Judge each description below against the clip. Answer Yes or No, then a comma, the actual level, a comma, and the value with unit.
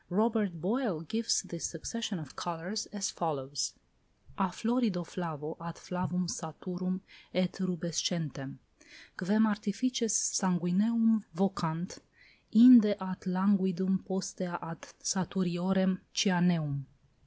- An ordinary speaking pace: No, slow, 95 wpm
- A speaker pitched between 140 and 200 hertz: Yes, medium, 185 Hz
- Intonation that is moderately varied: Yes, average, 3.2 semitones